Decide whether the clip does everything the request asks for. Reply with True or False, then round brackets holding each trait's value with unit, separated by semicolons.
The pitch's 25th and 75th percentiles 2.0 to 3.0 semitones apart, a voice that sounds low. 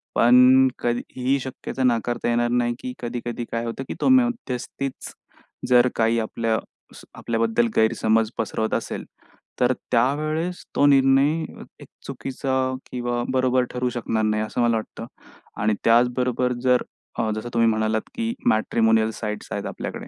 True (2.4 semitones; 120 Hz)